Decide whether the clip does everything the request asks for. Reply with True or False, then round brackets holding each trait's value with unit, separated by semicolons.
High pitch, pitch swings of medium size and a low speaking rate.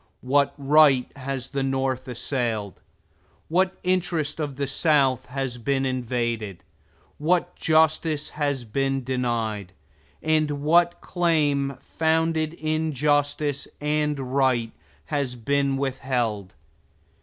False (140 Hz; 3.2 semitones; 105 wpm)